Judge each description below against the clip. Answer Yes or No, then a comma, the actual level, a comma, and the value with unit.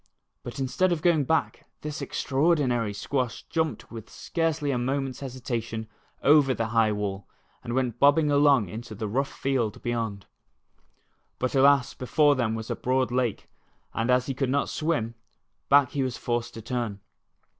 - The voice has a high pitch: No, low, 130 Hz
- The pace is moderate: Yes, average, 160 wpm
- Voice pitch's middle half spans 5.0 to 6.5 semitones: No, average, 3.7 semitones